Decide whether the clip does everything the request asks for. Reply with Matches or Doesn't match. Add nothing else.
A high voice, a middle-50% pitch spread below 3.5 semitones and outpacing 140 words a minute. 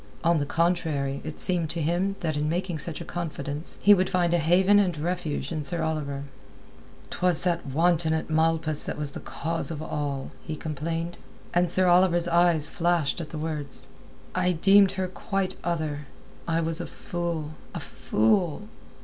Doesn't match